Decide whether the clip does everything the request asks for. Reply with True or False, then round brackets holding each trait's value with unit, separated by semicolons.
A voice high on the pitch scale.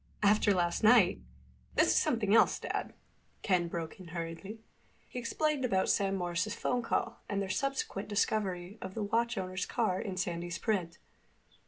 True (195 Hz)